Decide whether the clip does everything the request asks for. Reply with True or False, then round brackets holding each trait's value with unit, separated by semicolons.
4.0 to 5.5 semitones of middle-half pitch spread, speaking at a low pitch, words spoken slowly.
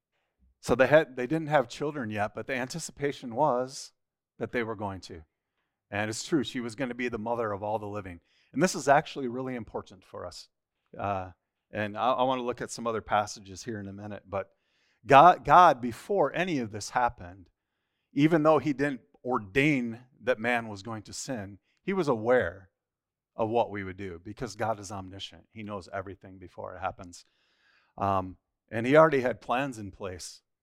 False (4.7 semitones; 115 Hz; 195 wpm)